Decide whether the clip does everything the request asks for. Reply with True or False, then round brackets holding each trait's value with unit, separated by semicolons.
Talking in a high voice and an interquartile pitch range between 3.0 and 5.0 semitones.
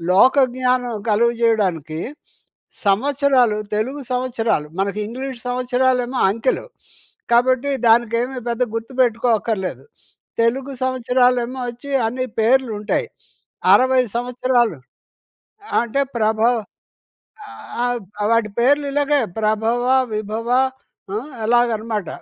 False (240 Hz; 2.6 semitones)